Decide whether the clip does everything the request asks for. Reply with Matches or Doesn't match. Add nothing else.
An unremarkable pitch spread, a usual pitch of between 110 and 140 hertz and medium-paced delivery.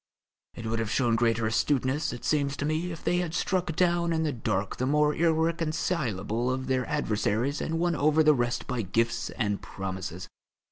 Doesn't match